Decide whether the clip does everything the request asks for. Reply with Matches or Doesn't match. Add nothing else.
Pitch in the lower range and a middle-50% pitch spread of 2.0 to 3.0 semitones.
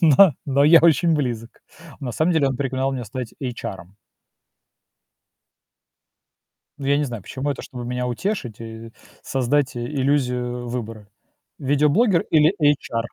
Doesn't match